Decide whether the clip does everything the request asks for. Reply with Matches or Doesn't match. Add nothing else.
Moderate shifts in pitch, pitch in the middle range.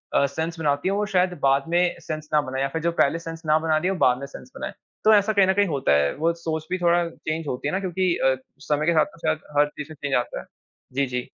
Matches